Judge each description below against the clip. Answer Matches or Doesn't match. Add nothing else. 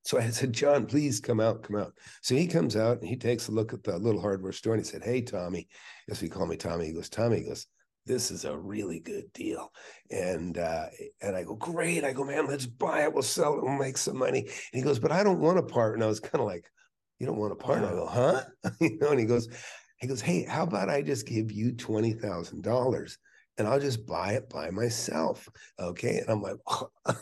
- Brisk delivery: Matches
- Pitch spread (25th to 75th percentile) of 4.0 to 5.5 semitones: Matches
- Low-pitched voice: Matches